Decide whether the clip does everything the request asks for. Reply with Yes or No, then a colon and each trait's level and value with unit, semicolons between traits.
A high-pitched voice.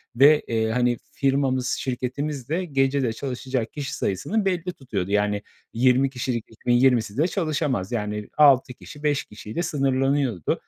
No: low, 130 Hz